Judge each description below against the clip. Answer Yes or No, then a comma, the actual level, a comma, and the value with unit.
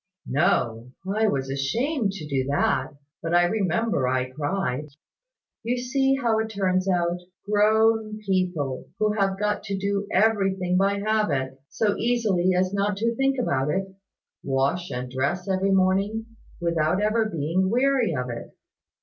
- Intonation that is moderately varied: No, wide, 5.9 semitones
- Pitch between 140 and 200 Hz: Yes, high, 190 Hz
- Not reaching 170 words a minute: Yes, average, 150 wpm